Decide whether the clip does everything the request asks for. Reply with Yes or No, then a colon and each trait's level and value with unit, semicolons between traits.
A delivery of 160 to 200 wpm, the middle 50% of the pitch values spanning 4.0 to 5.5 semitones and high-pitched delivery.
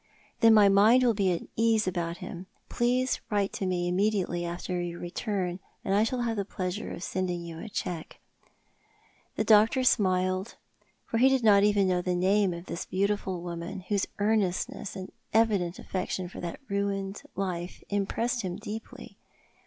No: average, 170 wpm; average, 3.0 semitones; high, 195 Hz